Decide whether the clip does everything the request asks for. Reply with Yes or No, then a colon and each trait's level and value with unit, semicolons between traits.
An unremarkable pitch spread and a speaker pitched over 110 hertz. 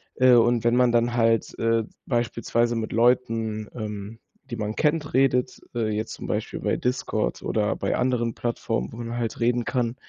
No: narrow, 1.6 semitones; low, 120 Hz